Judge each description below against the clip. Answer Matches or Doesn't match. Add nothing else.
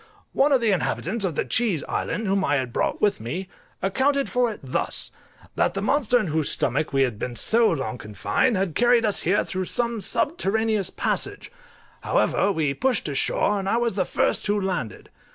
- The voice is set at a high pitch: Matches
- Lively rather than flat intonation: Matches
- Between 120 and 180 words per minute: Doesn't match